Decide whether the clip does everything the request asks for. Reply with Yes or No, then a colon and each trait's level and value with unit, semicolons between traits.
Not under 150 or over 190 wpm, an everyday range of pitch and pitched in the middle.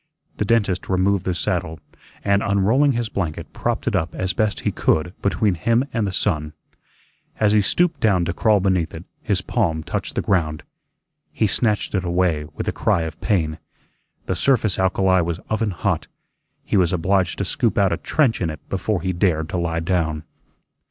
No: average, 185 wpm; average, 3.6 semitones; very low, 95 Hz